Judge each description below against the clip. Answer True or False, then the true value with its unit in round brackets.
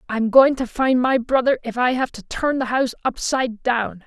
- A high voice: True (250 Hz)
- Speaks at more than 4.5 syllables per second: True (5.1 syllables/s)